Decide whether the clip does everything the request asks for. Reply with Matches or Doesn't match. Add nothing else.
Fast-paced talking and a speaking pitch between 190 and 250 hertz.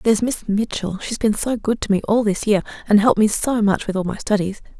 Matches